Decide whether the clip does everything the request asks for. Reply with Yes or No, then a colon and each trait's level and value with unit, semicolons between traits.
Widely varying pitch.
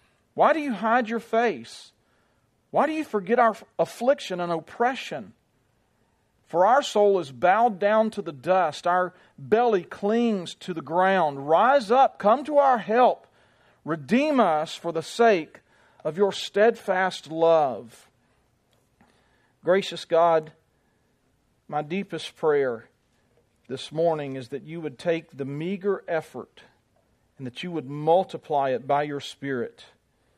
Yes: wide, 6.5 semitones